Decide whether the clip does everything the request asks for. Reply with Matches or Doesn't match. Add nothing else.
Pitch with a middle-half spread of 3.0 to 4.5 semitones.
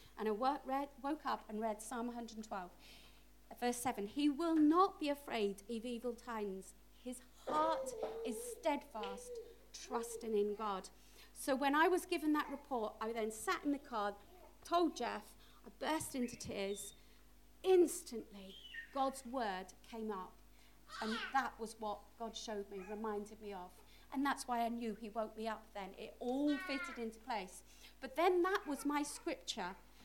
Doesn't match